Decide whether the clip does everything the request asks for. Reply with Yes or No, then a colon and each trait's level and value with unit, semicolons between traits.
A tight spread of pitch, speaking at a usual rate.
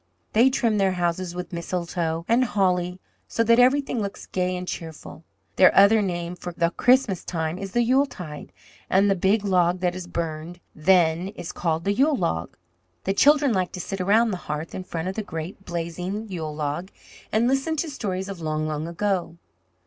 No: average, 3.6 semitones; average, 185 wpm